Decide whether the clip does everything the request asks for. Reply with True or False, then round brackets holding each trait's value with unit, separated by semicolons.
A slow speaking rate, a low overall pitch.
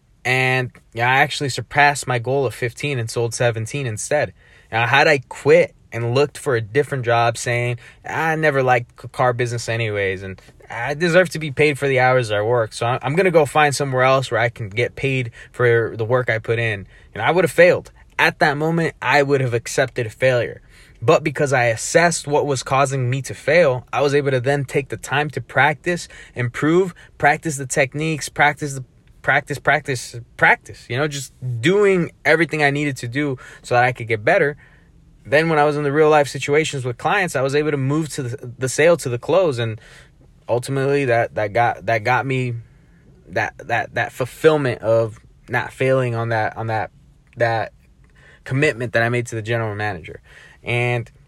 False (200 wpm; 130 Hz)